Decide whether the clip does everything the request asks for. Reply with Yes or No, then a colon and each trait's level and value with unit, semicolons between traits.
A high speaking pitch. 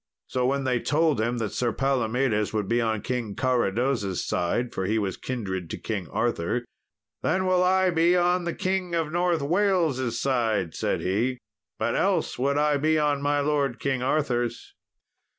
No: low, 130 Hz